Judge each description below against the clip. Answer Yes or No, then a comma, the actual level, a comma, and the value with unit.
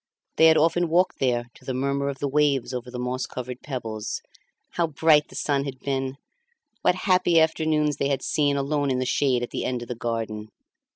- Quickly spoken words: Yes, fast, 210 wpm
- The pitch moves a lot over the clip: No, average, 3.1 semitones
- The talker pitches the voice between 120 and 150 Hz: Yes, medium, 140 Hz